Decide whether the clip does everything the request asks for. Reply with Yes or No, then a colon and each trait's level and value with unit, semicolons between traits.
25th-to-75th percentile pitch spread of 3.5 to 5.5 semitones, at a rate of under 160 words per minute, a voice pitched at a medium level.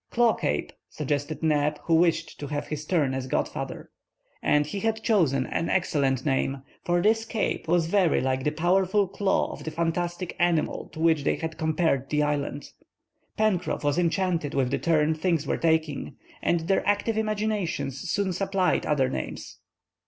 No: average, 4.3 semitones; average, 165 wpm; medium, 165 Hz